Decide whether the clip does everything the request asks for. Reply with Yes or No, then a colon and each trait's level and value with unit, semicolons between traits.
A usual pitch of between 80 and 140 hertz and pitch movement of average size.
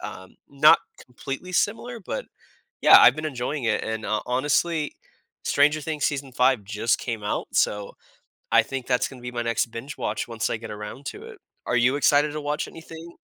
Yes: low, 135 Hz; average, 4.6 semitones